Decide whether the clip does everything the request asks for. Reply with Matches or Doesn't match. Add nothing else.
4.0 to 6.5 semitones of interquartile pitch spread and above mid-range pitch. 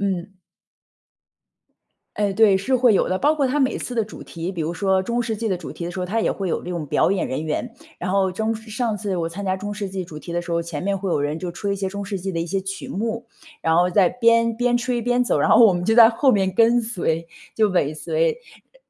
Matches